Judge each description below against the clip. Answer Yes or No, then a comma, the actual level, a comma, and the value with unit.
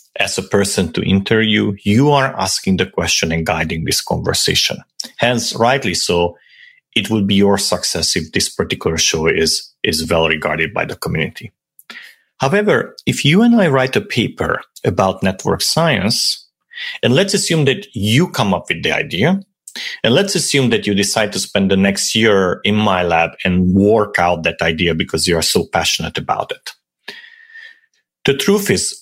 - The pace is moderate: Yes, average, 170 wpm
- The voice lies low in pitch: Yes, low, 105 Hz